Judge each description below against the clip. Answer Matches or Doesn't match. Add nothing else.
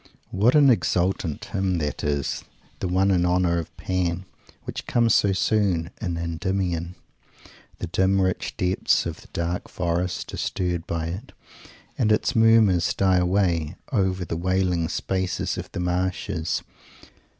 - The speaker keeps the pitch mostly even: Matches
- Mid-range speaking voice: Doesn't match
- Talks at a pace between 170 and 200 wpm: Doesn't match